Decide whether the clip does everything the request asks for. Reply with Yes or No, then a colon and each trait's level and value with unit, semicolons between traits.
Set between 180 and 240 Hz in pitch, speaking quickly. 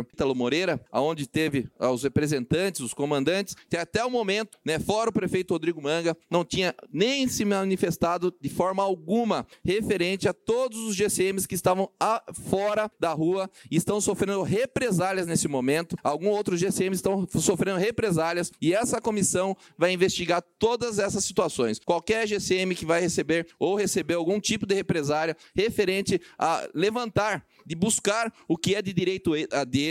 No: medium, 185 Hz; average, 160 wpm